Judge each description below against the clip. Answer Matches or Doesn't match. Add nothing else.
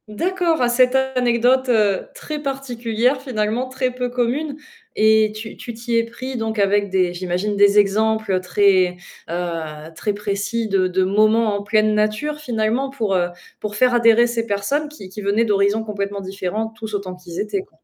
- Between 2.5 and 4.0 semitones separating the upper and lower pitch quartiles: Matches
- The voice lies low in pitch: Doesn't match